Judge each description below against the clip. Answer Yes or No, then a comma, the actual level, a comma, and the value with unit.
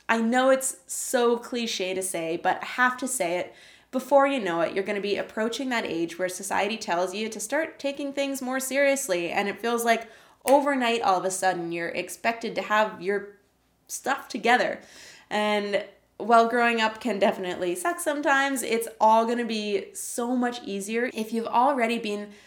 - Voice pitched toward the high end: Yes, high, 225 Hz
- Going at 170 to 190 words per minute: Yes, average, 185 wpm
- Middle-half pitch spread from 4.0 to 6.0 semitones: Yes, average, 4.5 semitones